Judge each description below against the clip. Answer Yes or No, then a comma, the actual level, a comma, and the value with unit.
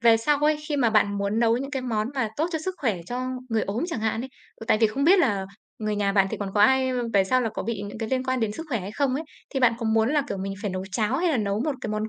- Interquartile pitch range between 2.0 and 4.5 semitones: Yes, average, 4.0 semitones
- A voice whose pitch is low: No, high, 225 Hz